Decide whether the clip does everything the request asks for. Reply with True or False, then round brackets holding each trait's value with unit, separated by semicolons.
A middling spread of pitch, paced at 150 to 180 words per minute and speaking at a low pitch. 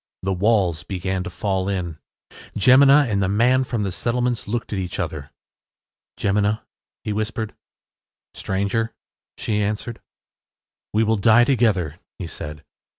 False (3.6 semitones; 135 wpm; 105 Hz)